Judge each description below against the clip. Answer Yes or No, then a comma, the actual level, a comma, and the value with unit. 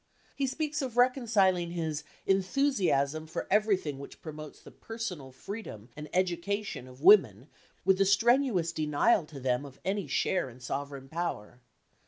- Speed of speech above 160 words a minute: No, average, 145 wpm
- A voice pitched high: No, medium, 175 Hz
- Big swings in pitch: Yes, wide, 6.7 semitones